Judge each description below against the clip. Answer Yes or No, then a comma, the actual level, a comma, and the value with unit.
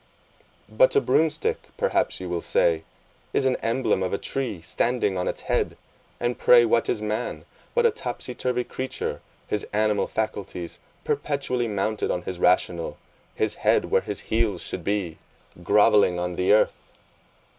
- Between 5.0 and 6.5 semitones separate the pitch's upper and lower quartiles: Yes, average, 5.3 semitones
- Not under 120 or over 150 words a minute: No, average, 160 wpm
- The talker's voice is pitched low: Yes, low, 105 Hz